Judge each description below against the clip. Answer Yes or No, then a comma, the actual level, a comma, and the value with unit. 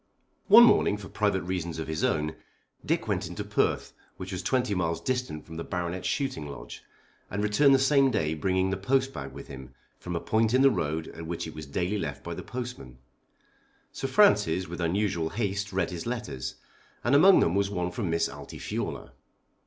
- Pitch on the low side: Yes, very low, 95 Hz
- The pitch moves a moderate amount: No, wide, 5.7 semitones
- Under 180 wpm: No, average, 190 wpm